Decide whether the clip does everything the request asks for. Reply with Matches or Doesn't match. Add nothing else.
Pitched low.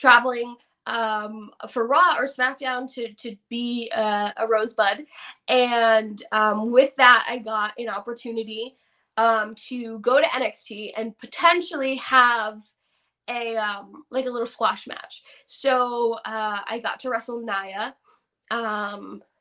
Doesn't match